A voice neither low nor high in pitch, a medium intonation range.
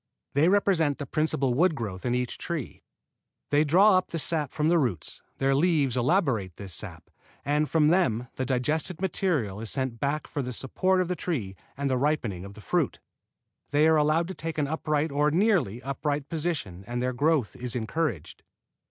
Yes: medium, 145 Hz; average, 4.6 semitones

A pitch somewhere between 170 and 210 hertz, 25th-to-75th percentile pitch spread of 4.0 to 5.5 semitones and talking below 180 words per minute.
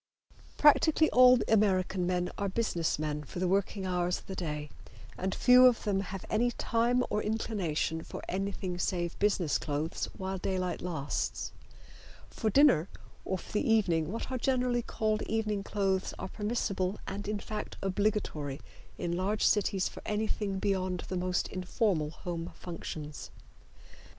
No: high, 190 Hz; average, 3.3 semitones; average, 150 wpm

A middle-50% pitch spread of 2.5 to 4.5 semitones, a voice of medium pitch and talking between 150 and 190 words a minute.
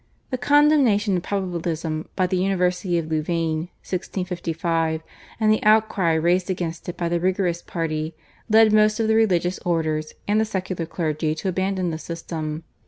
Yes: average, 3.2 semitones; medium, 175 Hz; average, 160 wpm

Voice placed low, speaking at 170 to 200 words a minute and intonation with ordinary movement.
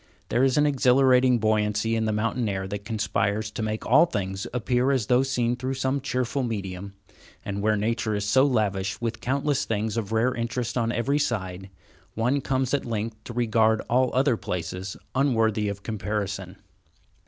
Yes: low, 115 Hz; average, 175 wpm; average, 3.5 semitones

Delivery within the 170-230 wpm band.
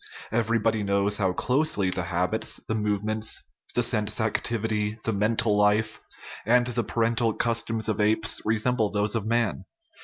No: average, 145 wpm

